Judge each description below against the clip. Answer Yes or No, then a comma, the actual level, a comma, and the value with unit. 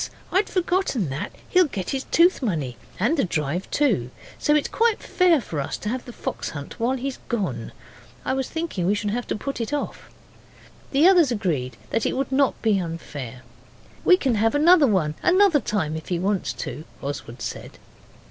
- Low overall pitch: No, high, 225 Hz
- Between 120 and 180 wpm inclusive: No, average, 190 wpm